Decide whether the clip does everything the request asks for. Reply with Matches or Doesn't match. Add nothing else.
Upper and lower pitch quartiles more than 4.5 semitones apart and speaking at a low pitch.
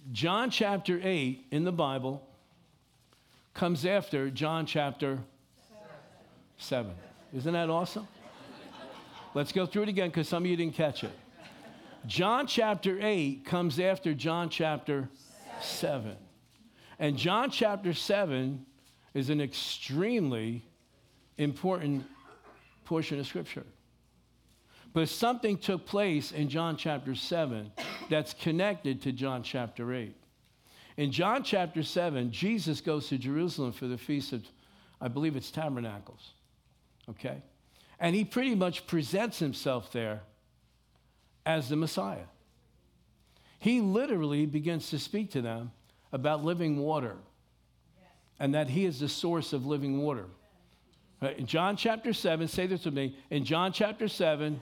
Doesn't match